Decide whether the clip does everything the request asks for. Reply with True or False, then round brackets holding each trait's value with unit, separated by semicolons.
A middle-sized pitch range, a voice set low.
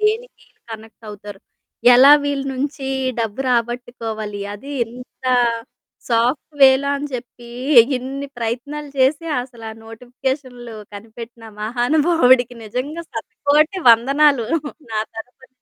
False (3.6 semitones; 250 Hz)